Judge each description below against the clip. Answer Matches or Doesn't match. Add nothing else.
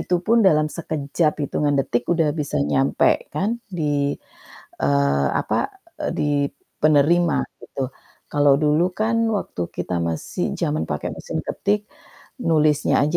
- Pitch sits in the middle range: Matches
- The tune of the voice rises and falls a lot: Matches